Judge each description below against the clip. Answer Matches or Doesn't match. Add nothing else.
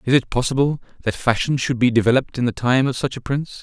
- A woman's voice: Doesn't match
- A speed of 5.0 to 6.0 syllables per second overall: Doesn't match